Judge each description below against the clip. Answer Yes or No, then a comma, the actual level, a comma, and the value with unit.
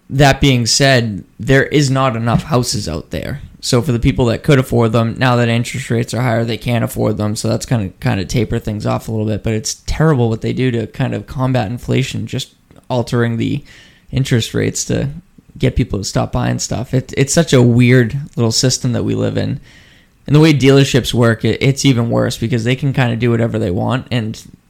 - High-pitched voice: No, low, 120 Hz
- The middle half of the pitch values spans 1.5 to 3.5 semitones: Yes, average, 2.7 semitones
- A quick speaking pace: Yes, fast, 225 wpm